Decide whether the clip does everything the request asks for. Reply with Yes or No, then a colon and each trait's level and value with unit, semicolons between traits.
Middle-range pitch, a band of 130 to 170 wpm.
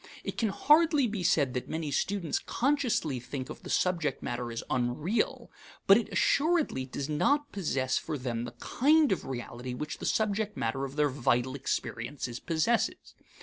Yes: medium, 150 Hz; average, 165 wpm